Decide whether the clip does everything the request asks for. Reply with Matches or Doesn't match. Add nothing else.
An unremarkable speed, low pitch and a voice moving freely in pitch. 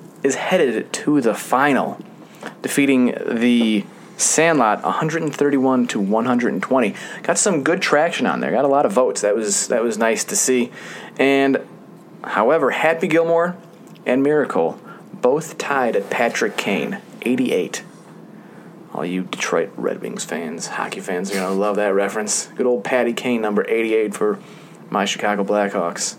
Matches